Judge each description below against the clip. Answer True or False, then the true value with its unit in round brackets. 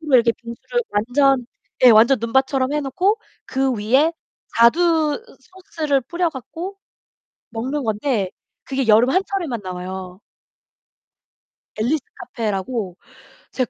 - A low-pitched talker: False (260 Hz)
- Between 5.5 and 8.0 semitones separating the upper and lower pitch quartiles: False (5.1 semitones)